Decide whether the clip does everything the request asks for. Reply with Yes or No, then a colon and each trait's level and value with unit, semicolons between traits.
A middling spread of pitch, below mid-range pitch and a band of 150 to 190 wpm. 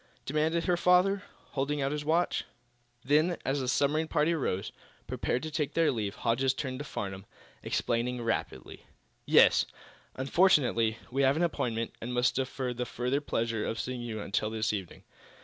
Yes: average, 4.7 semitones; low, 130 Hz; average, 165 wpm